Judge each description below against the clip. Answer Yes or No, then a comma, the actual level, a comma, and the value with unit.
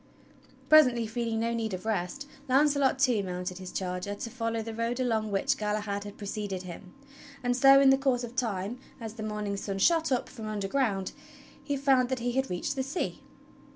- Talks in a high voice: Yes, high, 230 Hz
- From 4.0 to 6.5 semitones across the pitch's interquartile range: Yes, average, 4.3 semitones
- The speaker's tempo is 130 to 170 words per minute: No, average, 195 wpm